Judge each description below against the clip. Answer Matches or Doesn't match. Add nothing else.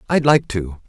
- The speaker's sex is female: Doesn't match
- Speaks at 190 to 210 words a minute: Matches